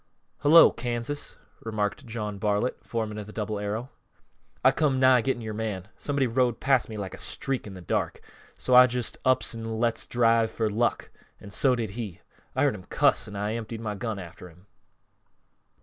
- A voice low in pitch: Yes, low, 115 Hz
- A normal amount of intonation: Yes, average, 3.0 semitones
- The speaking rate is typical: Yes, average, 190 wpm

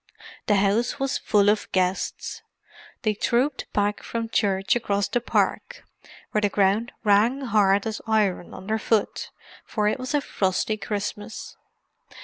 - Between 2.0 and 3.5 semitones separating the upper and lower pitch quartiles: Yes, narrow, 2.5 semitones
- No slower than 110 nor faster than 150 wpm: Yes, slow, 135 wpm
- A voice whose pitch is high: Yes, high, 210 Hz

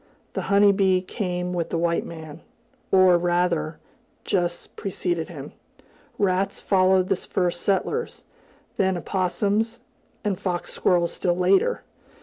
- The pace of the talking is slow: Yes, slow, 125 wpm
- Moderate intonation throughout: No, narrow, 2.0 semitones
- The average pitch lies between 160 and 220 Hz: Yes, medium, 185 Hz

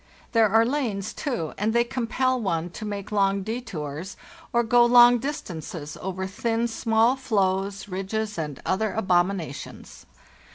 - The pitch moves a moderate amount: Yes, average, 4.0 semitones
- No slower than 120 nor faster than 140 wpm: Yes, slow, 135 wpm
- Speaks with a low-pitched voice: No, high, 210 Hz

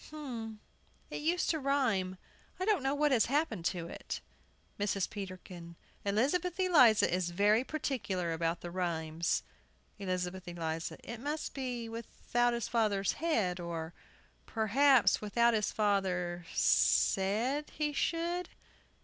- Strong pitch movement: Yes, wide, 7.3 semitones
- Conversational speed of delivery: No, slow, 125 wpm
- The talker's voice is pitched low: No, high, 215 Hz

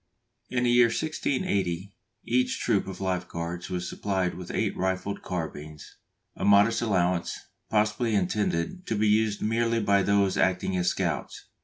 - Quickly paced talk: No, average, 150 wpm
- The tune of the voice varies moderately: Yes, average, 3.5 semitones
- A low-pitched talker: Yes, low, 100 Hz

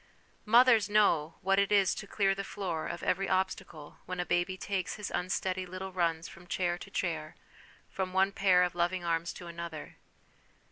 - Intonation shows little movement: Yes, narrow, 2.1 semitones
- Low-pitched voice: No, medium, 185 Hz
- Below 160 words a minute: No, average, 180 wpm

